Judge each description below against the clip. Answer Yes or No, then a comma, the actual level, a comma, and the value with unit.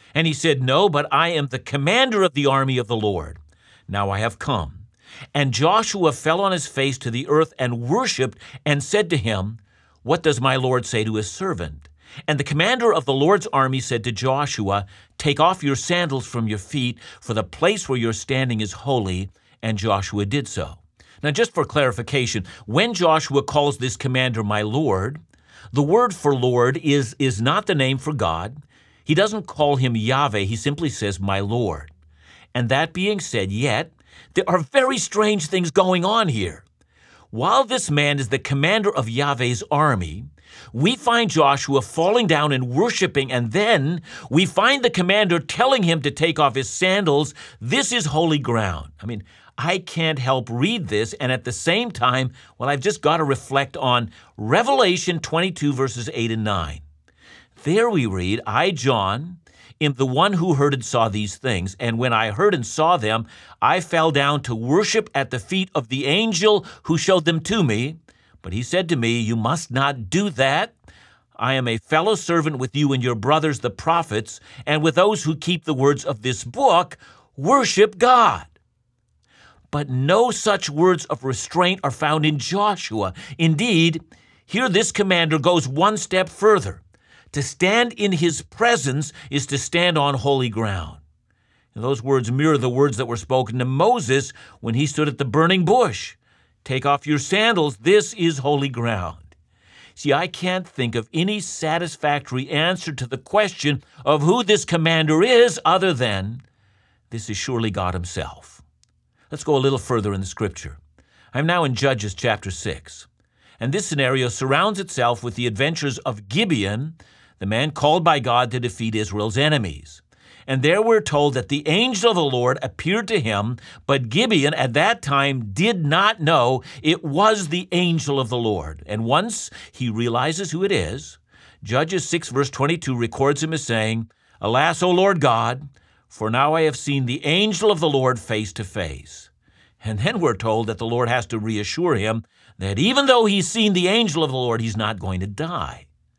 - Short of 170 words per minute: No, average, 180 wpm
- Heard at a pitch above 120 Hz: Yes, low, 135 Hz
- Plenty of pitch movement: Yes, wide, 6.3 semitones